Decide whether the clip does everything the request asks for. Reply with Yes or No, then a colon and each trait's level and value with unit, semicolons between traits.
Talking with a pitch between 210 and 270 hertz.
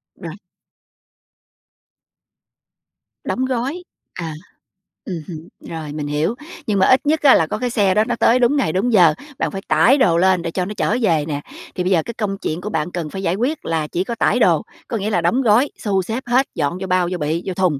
No: high, 190 Hz